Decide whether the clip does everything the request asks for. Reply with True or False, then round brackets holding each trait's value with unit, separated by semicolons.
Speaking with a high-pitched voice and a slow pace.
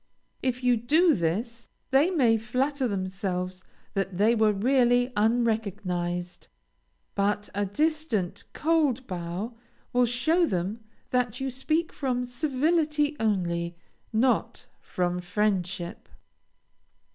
True (225 Hz; 105 wpm)